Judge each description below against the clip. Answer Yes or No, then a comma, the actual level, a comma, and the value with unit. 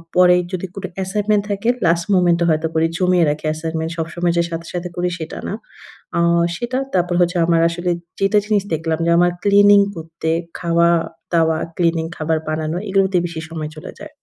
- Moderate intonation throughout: No, narrow, 2.2 semitones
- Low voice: No, medium, 170 Hz